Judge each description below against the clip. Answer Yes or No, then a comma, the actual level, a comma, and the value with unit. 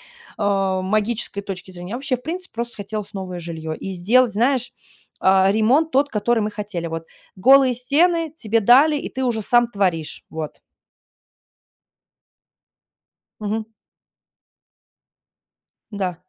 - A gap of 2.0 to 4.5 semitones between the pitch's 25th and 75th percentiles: No, average, 4.9 semitones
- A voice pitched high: Yes, high, 215 Hz